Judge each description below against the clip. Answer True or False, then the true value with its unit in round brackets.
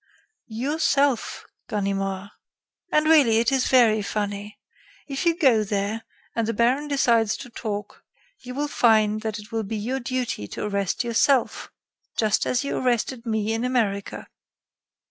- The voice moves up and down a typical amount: True (3.5 semitones)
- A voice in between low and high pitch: False (225 Hz)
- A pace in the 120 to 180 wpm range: True (145 wpm)